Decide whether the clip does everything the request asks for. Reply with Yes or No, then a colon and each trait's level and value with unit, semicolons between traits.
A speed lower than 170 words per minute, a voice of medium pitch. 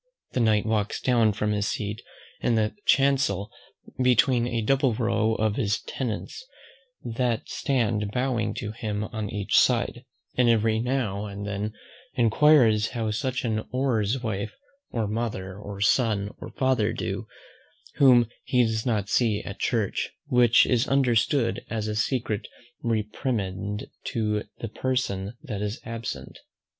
No: average, 140 wpm; low, 110 Hz